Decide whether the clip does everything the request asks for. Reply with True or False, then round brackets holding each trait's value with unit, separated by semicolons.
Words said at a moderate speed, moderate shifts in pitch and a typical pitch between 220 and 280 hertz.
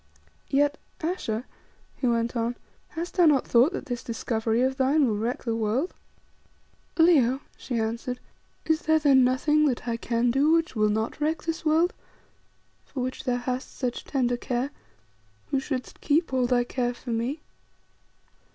True (160 wpm; 3.9 semitones; 255 Hz)